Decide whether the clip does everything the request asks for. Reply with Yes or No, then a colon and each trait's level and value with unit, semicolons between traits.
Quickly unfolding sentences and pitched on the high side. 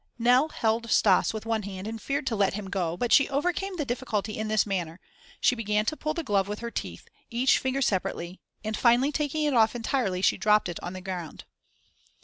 Yes: fast, 215 wpm; high, 220 Hz